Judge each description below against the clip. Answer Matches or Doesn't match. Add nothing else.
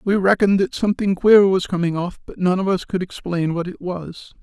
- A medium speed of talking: Doesn't match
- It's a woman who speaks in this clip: Doesn't match